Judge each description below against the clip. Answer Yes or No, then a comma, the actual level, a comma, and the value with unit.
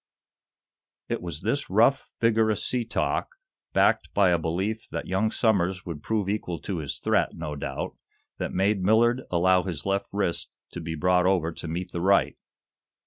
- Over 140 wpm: Yes, average, 170 wpm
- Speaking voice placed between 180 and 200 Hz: No, very low, 95 Hz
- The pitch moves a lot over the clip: No, average, 4.1 semitones